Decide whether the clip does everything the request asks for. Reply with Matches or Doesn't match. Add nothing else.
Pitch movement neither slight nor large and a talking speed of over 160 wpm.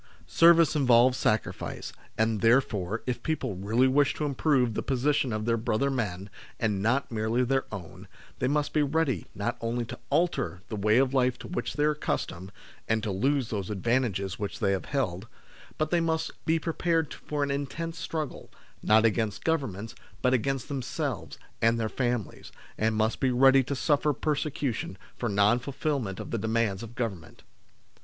Matches